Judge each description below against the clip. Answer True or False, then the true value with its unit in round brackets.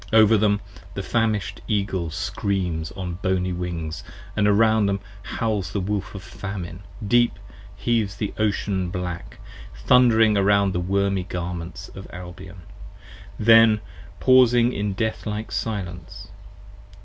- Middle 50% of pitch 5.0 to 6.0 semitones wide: False (3.3 semitones)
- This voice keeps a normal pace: False (125 wpm)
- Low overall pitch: True (100 Hz)